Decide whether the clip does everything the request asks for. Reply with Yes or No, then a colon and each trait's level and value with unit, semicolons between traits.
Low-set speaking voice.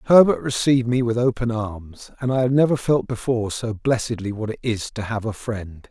Yes: low, 115 Hz